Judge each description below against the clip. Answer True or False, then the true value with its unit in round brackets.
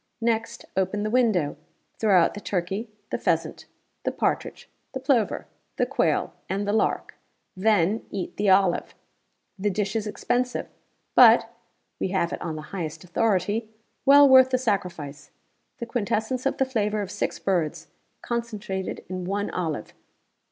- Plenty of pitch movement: False (3.9 semitones)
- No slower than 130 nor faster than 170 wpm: True (150 wpm)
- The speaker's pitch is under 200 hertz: False (205 Hz)